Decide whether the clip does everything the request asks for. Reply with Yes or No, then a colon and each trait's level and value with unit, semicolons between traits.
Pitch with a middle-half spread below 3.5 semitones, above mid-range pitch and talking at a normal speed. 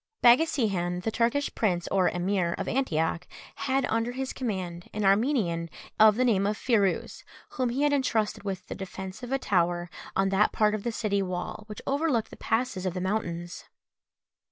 No: average, 4.9 semitones; high, 210 Hz; average, 180 wpm